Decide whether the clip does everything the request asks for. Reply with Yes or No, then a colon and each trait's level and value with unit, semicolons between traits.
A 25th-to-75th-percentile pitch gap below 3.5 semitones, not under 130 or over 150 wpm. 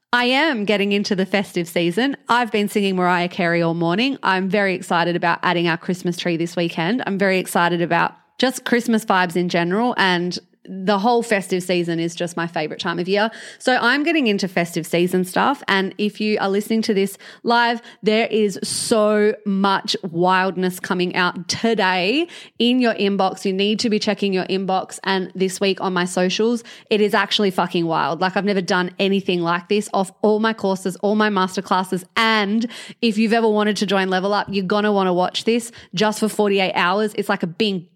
No: average, 2.9 semitones; average, 200 wpm